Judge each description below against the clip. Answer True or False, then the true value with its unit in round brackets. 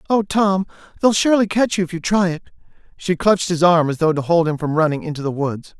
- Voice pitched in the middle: True (175 Hz)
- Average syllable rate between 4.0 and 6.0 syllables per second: False (6.2 syllables/s)